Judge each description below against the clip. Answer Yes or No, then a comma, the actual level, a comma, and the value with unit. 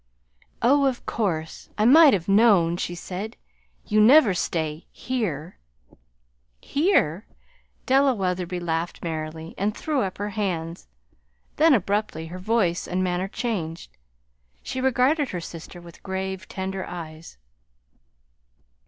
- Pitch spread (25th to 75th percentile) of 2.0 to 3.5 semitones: No, average, 5.3 semitones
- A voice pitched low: No, high, 190 Hz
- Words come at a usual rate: No, slow, 120 wpm